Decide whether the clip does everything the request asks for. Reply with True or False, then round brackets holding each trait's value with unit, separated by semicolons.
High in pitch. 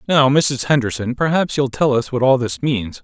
False (130 Hz)